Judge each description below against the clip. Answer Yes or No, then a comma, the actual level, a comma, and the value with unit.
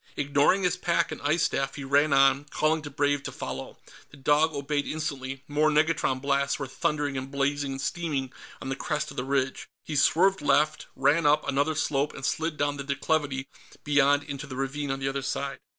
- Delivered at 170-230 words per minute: Yes, average, 200 wpm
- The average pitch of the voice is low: No, medium, 145 Hz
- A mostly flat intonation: Yes, narrow, 1.8 semitones